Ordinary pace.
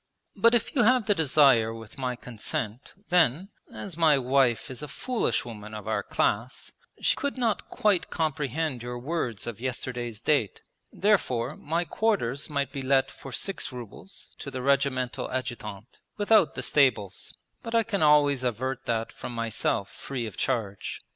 Yes: average, 160 wpm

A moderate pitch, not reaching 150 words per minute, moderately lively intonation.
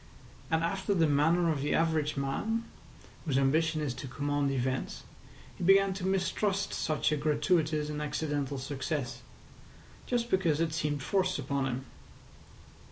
Yes: medium, 150 Hz; average, 140 wpm; average, 3.8 semitones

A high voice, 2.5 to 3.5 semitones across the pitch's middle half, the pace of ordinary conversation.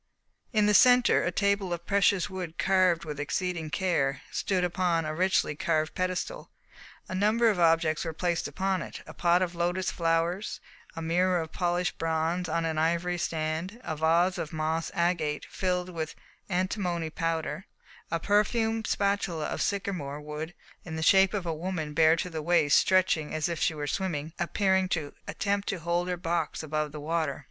No: medium, 175 Hz; average, 2.8 semitones; average, 180 wpm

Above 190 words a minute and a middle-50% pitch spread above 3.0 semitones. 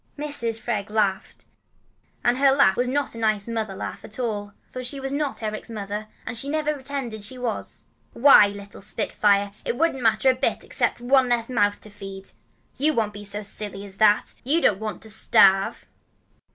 Yes: fast, 205 wpm; average, 4.0 semitones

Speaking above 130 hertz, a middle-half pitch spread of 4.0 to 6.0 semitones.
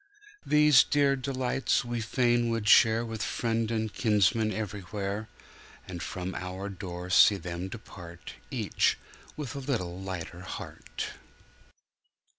No: low, 110 Hz; average, 4.3 semitones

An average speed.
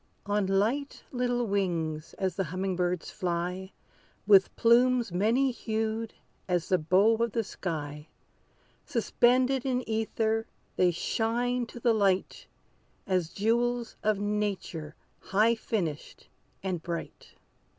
No: slow, 120 wpm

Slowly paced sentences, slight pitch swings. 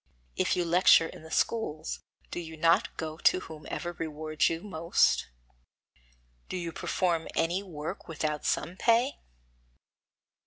Yes: slow, 130 wpm; narrow, 2.2 semitones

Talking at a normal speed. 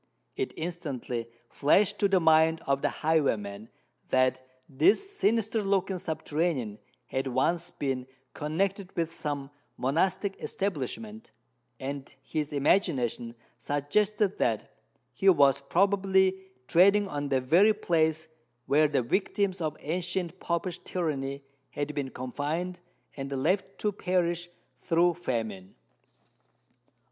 No: slow, 115 wpm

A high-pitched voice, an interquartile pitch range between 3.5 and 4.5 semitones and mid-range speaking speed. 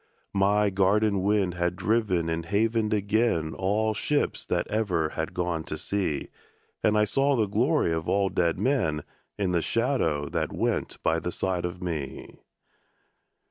No: very low, 95 Hz; average, 4.1 semitones; average, 155 wpm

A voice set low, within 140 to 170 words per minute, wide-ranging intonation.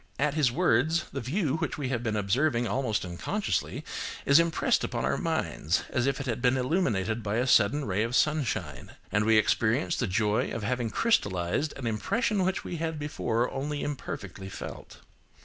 No: low, 125 Hz; average, 180 wpm; wide, 5.7 semitones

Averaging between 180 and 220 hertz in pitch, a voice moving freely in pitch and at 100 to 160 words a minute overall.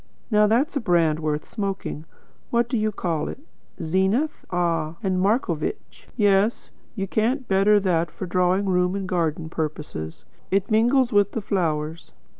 No: high, 190 Hz; average, 4.5 semitones; average, 150 wpm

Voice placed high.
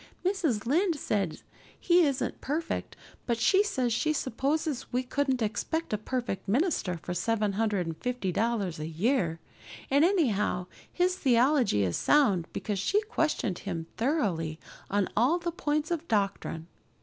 Yes: high, 245 Hz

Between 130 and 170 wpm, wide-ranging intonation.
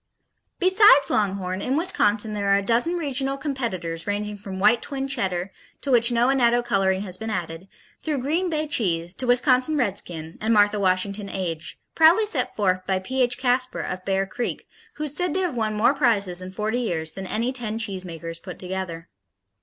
No: average, 185 wpm; wide, 5.7 semitones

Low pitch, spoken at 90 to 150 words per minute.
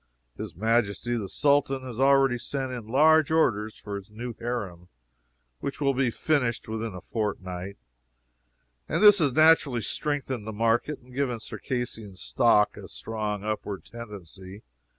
Yes: low, 115 Hz; average, 145 wpm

